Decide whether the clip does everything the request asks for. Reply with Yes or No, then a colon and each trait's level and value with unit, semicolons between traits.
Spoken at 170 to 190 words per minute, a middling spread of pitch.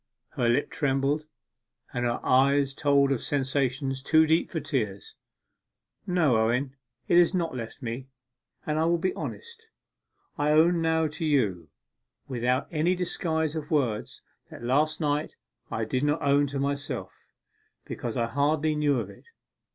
No: average, 150 wpm; average, 3.5 semitones